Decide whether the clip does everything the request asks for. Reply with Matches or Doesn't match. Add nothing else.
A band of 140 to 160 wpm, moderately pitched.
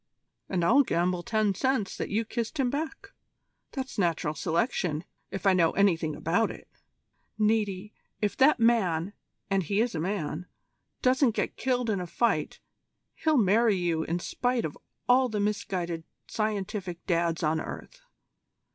Doesn't match